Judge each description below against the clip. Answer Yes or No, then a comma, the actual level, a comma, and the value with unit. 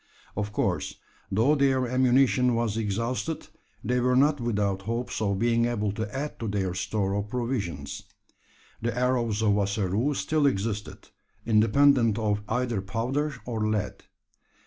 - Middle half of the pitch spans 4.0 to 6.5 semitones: No, average, 3.5 semitones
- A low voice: Yes, low, 115 Hz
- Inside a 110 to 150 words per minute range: Yes, average, 140 wpm